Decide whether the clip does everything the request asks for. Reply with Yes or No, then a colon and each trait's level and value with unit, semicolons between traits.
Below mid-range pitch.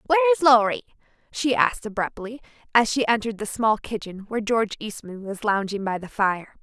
No: high, 225 Hz